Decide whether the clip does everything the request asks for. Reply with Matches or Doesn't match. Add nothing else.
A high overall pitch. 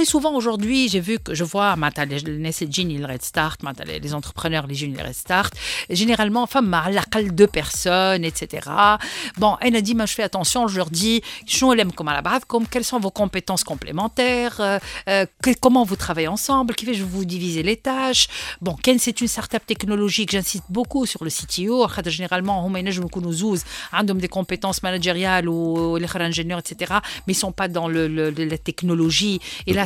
Matches